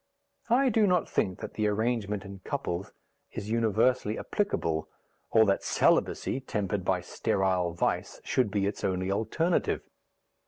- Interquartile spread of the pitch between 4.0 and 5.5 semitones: Yes, average, 4.5 semitones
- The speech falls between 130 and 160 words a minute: Yes, slow, 135 wpm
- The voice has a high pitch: No, low, 105 Hz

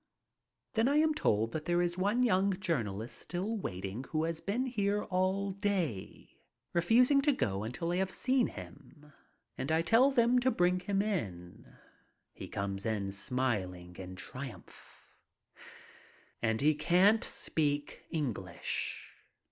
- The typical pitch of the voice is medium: Yes, medium, 170 Hz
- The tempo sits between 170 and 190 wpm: No, average, 140 wpm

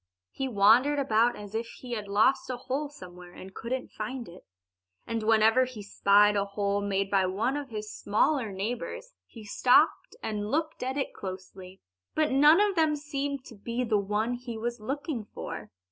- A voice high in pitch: Yes, high, 230 Hz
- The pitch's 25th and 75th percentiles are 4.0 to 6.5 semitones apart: Yes, average, 4.8 semitones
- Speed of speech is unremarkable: Yes, average, 180 wpm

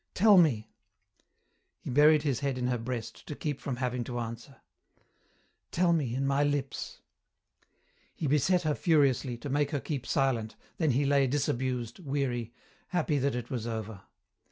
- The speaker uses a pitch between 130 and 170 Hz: Yes, low, 135 Hz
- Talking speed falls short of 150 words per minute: No, average, 160 wpm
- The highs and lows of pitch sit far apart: No, average, 3.2 semitones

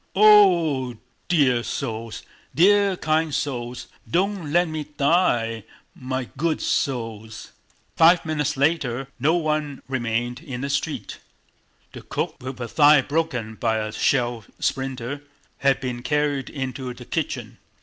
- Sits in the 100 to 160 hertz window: Yes, low, 135 Hz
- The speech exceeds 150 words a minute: No, slow, 135 wpm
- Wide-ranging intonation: No, average, 4.4 semitones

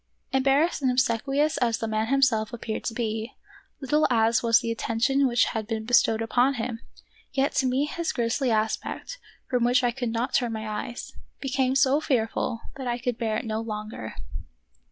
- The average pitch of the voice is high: Yes, high, 240 Hz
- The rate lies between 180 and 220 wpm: Yes, average, 185 wpm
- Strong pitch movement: No, average, 3.0 semitones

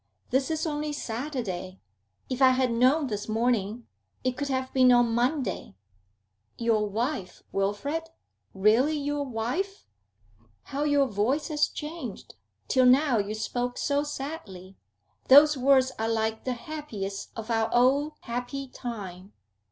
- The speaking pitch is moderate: No, very high, 250 Hz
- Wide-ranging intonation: No, average, 4.5 semitones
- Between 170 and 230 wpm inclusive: No, slow, 135 wpm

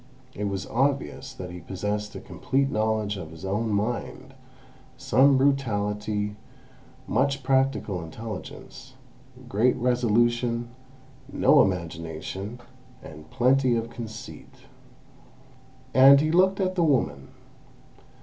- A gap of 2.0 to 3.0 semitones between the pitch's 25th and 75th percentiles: No, average, 4.8 semitones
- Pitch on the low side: Yes, low, 115 Hz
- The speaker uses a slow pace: Yes, slow, 105 wpm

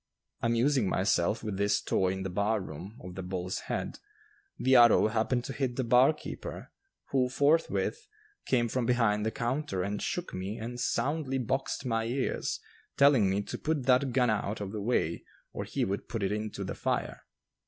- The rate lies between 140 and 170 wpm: No, average, 180 wpm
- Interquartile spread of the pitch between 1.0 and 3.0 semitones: No, average, 4.3 semitones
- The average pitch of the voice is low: Yes, low, 115 Hz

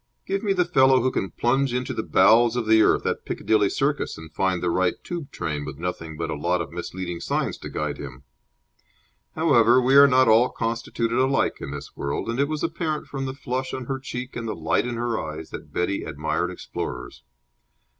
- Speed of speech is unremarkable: No, fast, 210 wpm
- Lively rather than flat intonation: Yes, wide, 7.2 semitones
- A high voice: No, low, 115 Hz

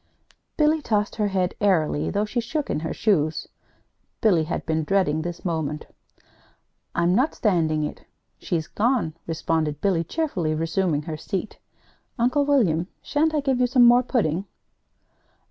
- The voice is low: No, high, 190 Hz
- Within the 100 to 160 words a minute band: Yes, average, 145 wpm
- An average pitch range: No, wide, 7.2 semitones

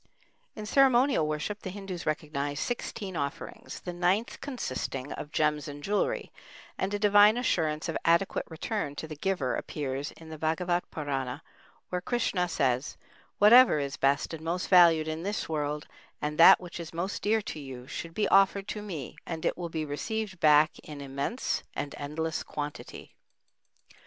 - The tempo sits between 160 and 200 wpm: Yes, average, 165 wpm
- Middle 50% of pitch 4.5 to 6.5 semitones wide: Yes, average, 4.9 semitones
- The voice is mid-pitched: Yes, medium, 165 Hz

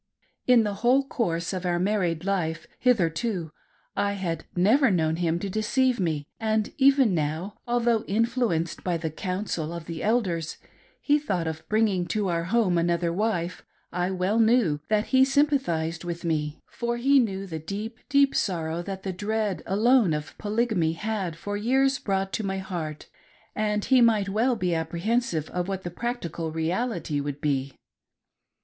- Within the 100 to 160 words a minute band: No, average, 170 wpm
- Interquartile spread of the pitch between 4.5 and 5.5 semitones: Yes, average, 5.2 semitones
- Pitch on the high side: Yes, high, 195 Hz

